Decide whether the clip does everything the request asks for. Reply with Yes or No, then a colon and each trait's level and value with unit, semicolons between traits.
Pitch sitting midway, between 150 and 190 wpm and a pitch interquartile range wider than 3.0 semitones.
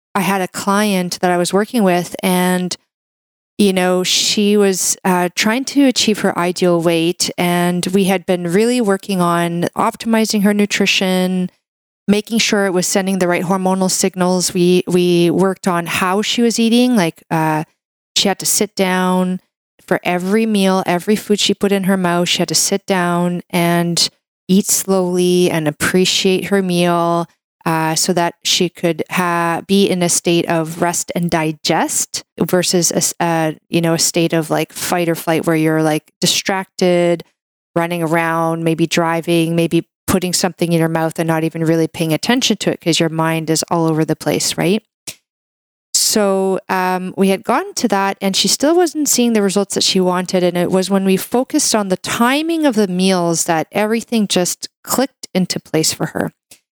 No: medium, 180 Hz; average, 180 wpm; average, 2.7 semitones